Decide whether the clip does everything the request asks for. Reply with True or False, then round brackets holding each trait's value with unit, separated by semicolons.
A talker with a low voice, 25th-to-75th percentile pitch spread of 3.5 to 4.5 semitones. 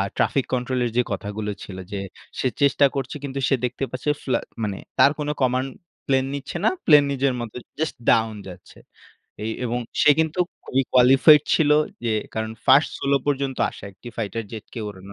True (130 Hz; 4.0 semitones)